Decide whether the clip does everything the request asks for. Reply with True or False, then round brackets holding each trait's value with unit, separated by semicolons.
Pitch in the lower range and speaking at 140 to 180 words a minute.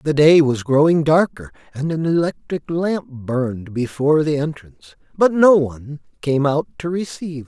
False (150 Hz; 170 wpm)